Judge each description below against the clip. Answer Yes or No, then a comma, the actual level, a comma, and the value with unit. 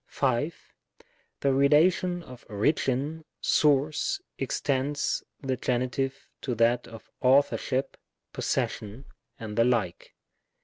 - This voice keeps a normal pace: No, slow, 100 wpm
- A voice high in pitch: No, low, 135 Hz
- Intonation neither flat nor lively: Yes, average, 3.3 semitones